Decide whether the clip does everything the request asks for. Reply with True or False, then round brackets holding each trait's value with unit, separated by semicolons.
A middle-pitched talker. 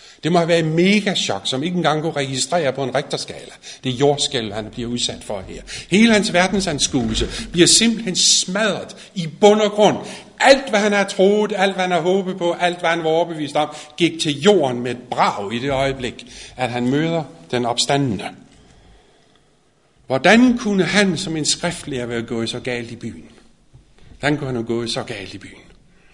True (160 Hz)